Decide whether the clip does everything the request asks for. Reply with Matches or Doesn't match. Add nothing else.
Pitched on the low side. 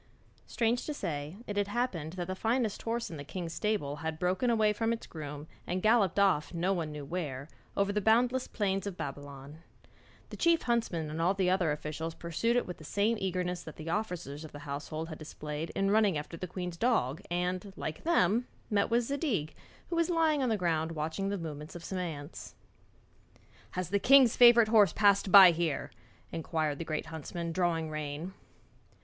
Doesn't match